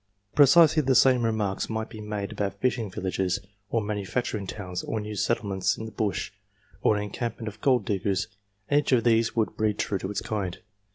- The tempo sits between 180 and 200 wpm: Yes, average, 190 wpm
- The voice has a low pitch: Yes, low, 105 Hz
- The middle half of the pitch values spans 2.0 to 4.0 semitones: Yes, average, 2.8 semitones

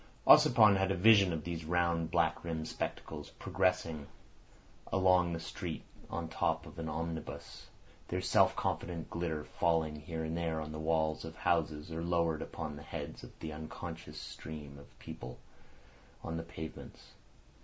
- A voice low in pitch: Yes, very low, 80 Hz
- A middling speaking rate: Yes, average, 160 wpm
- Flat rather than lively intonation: Yes, narrow, 1.6 semitones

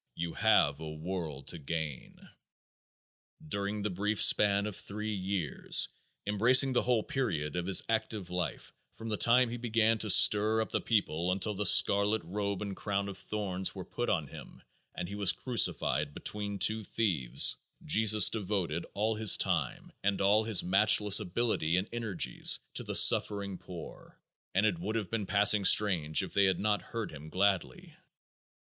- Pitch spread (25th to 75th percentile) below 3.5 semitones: Yes, average, 3.1 semitones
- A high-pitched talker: No, low, 100 Hz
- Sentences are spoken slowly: No, average, 165 wpm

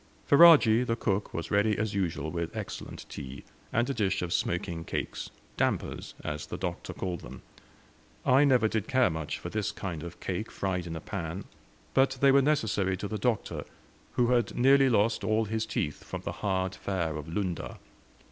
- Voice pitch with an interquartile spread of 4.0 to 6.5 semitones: Yes, wide, 5.4 semitones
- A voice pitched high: No, low, 100 Hz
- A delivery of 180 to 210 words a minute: Yes, average, 185 wpm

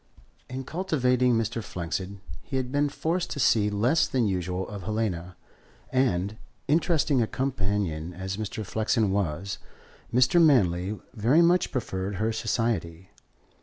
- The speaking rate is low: Yes, slow, 130 wpm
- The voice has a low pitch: Yes, low, 110 Hz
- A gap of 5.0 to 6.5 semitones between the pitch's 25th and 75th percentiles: Yes, wide, 5.5 semitones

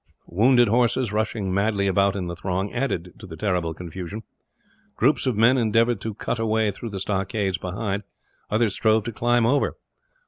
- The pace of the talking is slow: No, average, 175 wpm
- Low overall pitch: Yes, low, 105 Hz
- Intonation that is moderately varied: Yes, average, 3.3 semitones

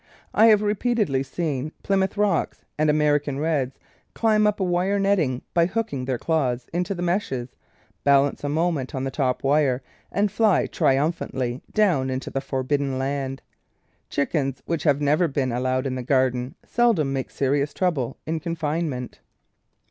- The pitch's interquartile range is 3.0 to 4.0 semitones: No, average, 5.0 semitones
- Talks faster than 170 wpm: No, average, 160 wpm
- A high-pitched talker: No, medium, 145 Hz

